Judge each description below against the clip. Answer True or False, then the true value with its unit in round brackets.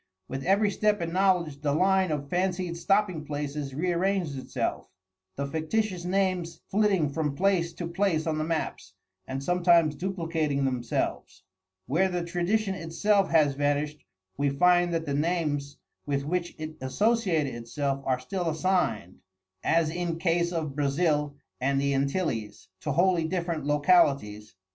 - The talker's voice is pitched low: False (165 Hz)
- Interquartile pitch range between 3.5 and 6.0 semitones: True (4.1 semitones)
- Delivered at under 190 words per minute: True (145 wpm)